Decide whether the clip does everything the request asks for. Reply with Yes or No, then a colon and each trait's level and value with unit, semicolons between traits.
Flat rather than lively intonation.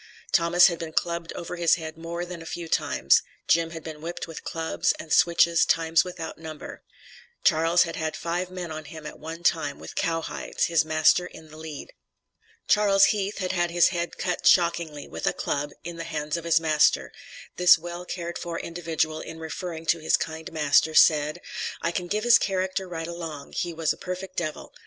Yes: narrow, 1.6 semitones